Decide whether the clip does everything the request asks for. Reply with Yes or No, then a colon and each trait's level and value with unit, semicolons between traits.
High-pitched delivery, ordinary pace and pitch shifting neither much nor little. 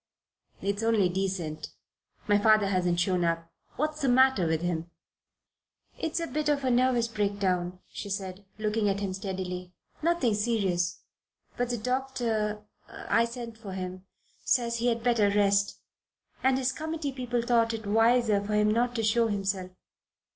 Yes: high, 215 Hz; average, 155 wpm; average, 4.0 semitones